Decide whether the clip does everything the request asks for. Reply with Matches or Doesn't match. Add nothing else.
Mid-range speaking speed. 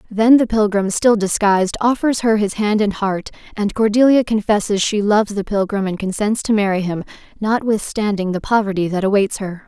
Matches